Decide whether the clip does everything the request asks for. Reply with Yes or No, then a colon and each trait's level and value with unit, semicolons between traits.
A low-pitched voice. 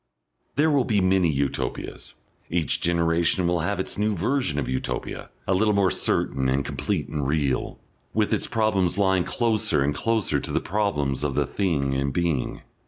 Yes: very low, 85 Hz